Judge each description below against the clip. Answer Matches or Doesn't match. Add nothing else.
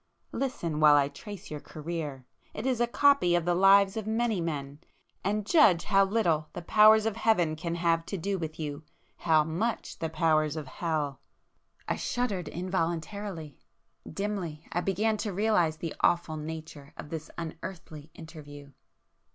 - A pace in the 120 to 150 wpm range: Matches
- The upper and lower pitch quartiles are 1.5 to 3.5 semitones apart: Doesn't match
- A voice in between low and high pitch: Matches